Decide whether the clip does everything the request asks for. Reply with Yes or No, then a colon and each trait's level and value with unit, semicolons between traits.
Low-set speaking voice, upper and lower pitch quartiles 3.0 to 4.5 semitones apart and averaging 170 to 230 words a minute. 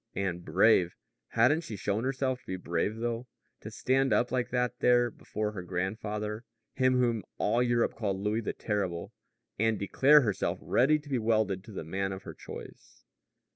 Yes: low, 110 Hz; average, 4.0 semitones; average, 175 wpm